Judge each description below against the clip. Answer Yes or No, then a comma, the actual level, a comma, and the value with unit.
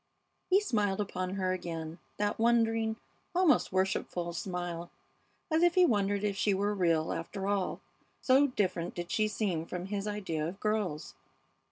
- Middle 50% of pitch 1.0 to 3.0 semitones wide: No, average, 3.4 semitones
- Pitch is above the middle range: Yes, high, 195 Hz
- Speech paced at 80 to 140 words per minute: No, average, 155 wpm